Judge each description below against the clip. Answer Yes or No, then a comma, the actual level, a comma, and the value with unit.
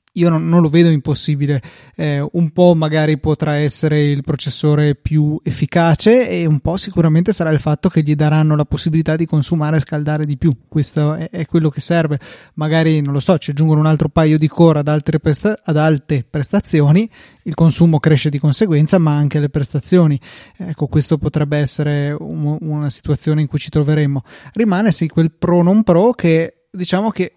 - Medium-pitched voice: Yes, medium, 155 Hz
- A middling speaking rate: No, fast, 190 wpm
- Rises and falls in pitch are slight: Yes, narrow, 1.9 semitones